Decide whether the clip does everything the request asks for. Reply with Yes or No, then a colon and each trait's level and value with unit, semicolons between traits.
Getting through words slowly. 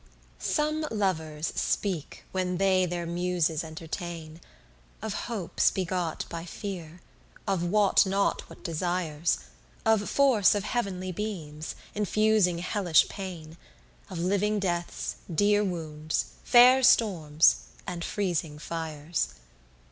Yes: slow, 110 wpm